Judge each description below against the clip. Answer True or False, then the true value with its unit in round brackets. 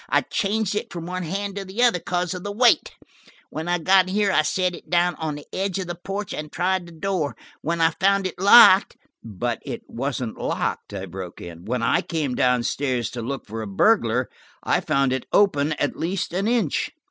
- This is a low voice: False (170 Hz)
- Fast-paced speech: True (215 wpm)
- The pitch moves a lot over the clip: True (6.7 semitones)